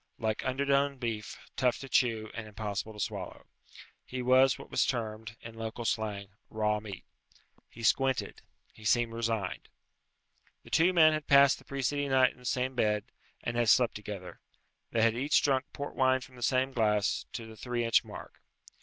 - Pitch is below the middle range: Yes, low, 120 Hz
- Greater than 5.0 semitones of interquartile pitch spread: No, average, 3.3 semitones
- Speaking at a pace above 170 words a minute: Yes, average, 180 wpm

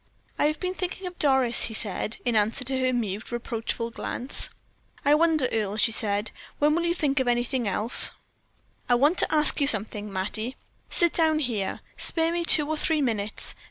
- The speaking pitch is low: No, very high, 255 Hz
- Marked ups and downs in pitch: Yes, wide, 5.7 semitones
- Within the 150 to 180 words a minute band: No, average, 190 wpm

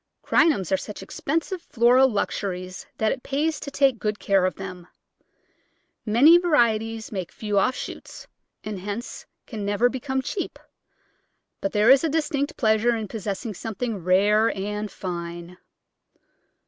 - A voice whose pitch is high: Yes, high, 220 Hz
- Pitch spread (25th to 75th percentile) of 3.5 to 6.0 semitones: Yes, average, 4.9 semitones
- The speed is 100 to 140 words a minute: Yes, slow, 135 wpm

